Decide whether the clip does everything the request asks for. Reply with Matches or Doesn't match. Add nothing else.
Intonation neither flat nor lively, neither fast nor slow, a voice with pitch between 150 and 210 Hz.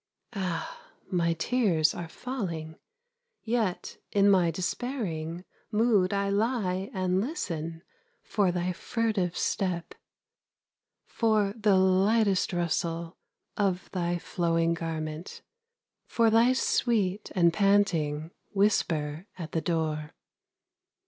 Doesn't match